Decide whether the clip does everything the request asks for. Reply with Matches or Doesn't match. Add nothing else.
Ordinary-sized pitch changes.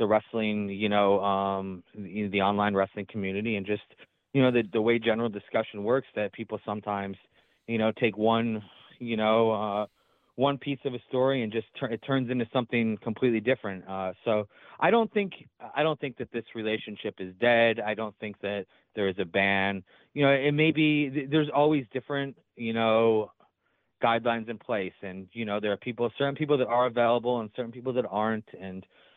Matches